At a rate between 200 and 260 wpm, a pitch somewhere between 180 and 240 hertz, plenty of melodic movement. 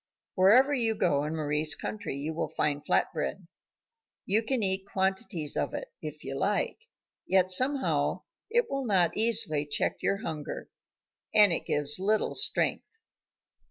No: average, 150 wpm; high, 190 Hz; wide, 6.5 semitones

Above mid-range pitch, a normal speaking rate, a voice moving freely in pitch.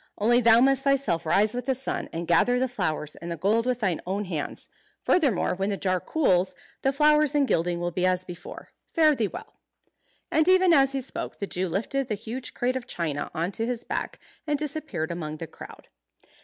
No: high, 220 Hz; fast, 210 wpm; wide, 7.3 semitones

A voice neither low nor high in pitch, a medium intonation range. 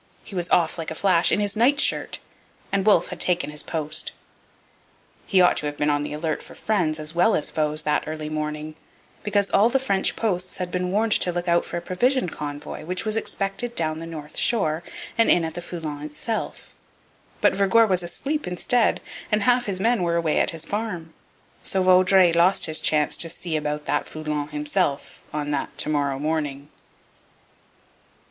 Yes: medium, 170 Hz; average, 4.4 semitones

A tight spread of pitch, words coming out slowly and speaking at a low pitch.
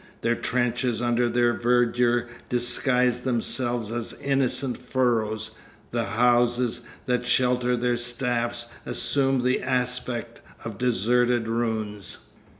Yes: narrow, 0.9 semitones; slow, 105 wpm; low, 120 Hz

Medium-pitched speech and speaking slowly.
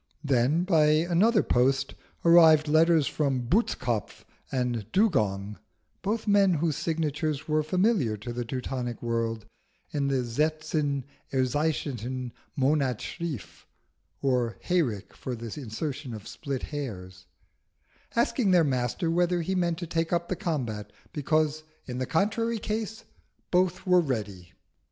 Yes: medium, 145 Hz; slow, 130 wpm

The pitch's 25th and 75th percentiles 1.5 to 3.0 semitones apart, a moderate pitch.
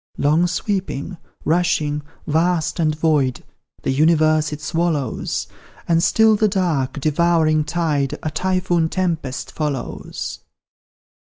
Yes: average, 2.7 semitones; medium, 160 Hz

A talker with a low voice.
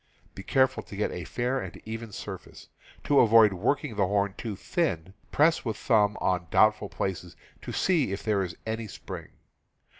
Yes: low, 105 Hz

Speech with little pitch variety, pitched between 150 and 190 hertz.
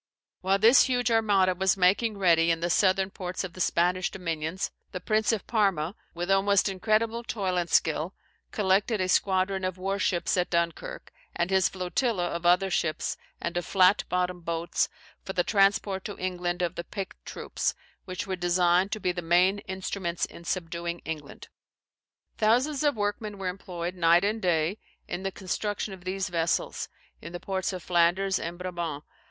Yes: narrow, 2.2 semitones; medium, 185 Hz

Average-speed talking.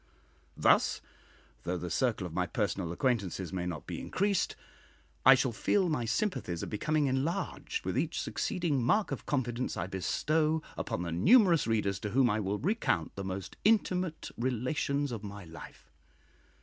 Yes: average, 160 wpm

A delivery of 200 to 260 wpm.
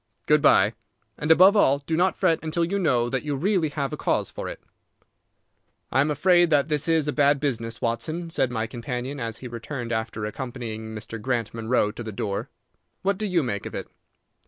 Yes: fast, 205 wpm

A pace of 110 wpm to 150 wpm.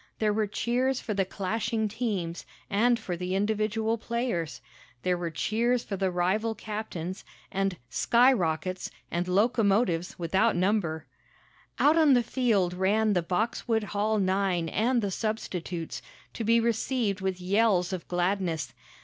Yes: average, 140 wpm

